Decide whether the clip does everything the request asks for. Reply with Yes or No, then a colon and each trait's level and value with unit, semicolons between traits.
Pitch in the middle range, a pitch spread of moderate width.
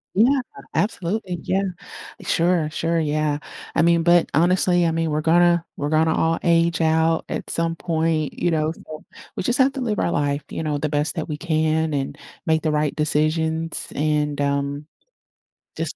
No: medium, 160 Hz; narrow, 1.9 semitones